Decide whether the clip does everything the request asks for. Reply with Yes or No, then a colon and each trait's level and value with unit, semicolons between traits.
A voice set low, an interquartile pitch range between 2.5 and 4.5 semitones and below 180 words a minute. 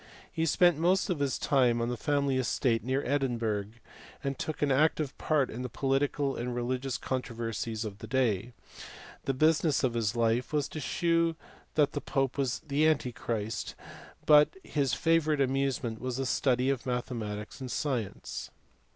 Yes: low, 130 Hz; average, 3.5 semitones; average, 160 wpm